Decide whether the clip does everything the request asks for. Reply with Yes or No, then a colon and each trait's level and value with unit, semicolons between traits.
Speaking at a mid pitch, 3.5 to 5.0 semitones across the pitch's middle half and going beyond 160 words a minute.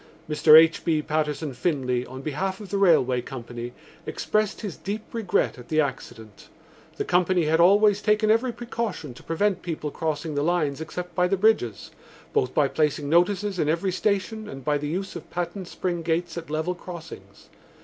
Yes: medium, 170 Hz; average, 4.6 semitones; average, 180 wpm